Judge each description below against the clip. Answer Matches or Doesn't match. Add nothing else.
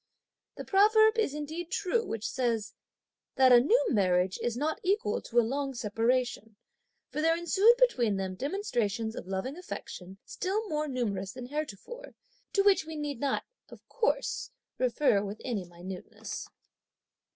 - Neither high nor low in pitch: Doesn't match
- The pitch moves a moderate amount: Doesn't match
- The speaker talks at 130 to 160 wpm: Matches